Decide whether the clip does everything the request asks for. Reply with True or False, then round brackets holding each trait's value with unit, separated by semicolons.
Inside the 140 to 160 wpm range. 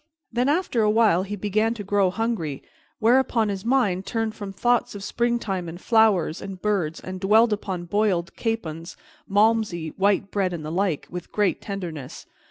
False (170 wpm)